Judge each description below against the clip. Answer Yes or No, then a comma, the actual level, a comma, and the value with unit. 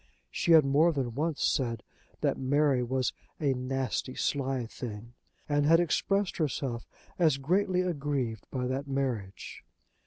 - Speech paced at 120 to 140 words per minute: Yes, slow, 135 wpm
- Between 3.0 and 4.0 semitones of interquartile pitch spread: Yes, average, 3.3 semitones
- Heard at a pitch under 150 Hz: Yes, low, 135 Hz